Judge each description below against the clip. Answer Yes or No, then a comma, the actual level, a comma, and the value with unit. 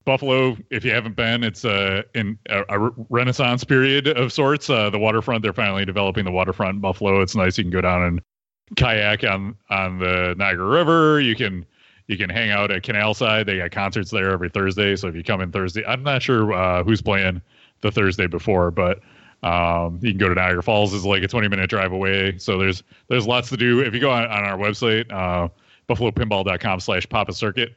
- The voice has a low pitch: Yes, low, 105 Hz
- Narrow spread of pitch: No, average, 3.6 semitones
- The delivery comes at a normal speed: No, fast, 215 wpm